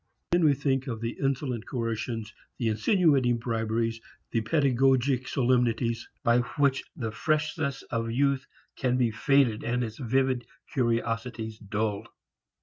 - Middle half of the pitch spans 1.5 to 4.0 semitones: Yes, average, 2.9 semitones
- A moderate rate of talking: No, slow, 130 wpm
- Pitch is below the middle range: Yes, low, 120 Hz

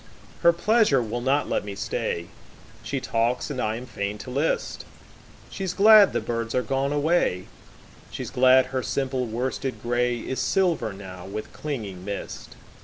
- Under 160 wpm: Yes, average, 140 wpm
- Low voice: Yes, low, 125 Hz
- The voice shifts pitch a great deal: No, average, 4.7 semitones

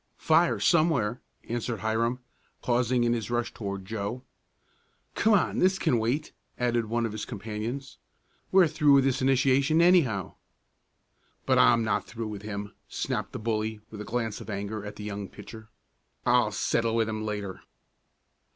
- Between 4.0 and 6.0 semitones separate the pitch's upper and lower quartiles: No, average, 3.6 semitones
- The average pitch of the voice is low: Yes, low, 115 Hz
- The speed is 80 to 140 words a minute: No, average, 160 wpm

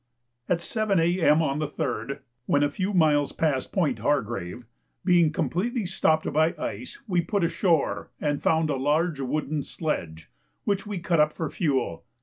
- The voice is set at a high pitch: No, medium, 155 Hz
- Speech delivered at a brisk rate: No, average, 160 wpm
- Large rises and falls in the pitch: No, average, 3.5 semitones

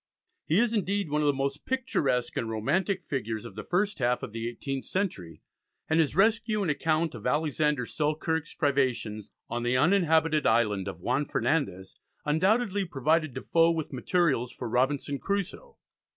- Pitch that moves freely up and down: Yes, wide, 6.3 semitones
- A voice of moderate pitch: Yes, medium, 150 Hz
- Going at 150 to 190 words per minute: Yes, average, 160 wpm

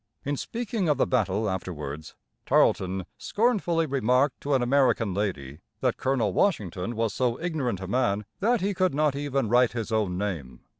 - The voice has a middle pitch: No, low, 120 Hz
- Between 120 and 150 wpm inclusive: No, average, 165 wpm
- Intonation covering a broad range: Yes, wide, 6.9 semitones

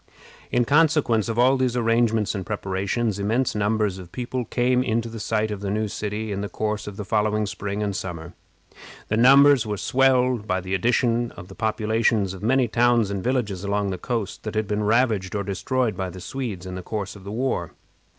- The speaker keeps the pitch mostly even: No, average, 3.3 semitones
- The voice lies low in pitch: Yes, low, 110 Hz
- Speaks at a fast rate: Yes, fast, 210 wpm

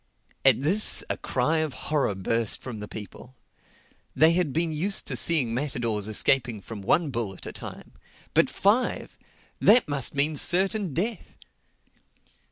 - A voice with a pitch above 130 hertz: Yes, medium, 140 Hz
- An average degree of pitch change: No, wide, 6.4 semitones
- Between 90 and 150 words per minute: Yes, average, 145 wpm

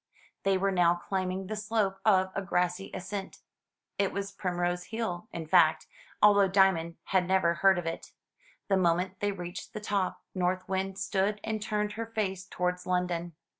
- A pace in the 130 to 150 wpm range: No, average, 170 wpm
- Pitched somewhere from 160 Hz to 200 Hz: Yes, high, 190 Hz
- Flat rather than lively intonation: Yes, narrow, 2.0 semitones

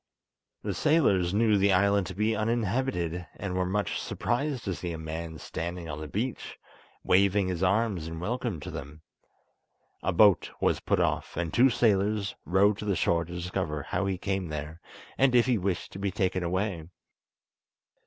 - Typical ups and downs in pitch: Yes, average, 3.6 semitones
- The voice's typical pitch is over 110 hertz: No, very low, 95 Hz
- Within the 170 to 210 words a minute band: Yes, average, 175 wpm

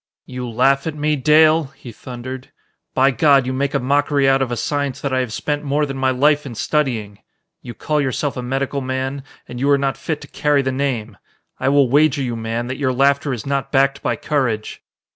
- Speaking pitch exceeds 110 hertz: Yes, low, 135 Hz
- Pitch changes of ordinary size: No, narrow, 2.2 semitones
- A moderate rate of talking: No, fast, 220 wpm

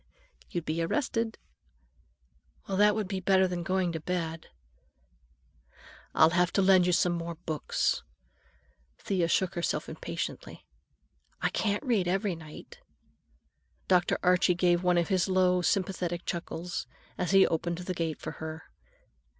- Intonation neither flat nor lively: No, narrow, 2.0 semitones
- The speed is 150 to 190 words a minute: No, average, 140 wpm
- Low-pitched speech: No, medium, 180 Hz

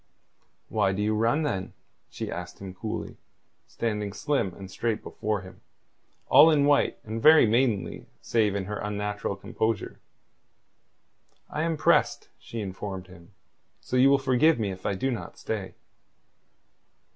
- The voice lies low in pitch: Yes, low, 105 Hz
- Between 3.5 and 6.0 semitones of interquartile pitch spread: Yes, average, 4.6 semitones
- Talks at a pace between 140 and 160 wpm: Yes, average, 145 wpm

